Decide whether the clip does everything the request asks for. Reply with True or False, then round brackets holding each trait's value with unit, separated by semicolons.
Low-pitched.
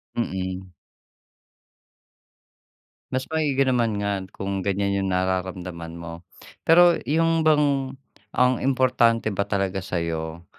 True (100 Hz)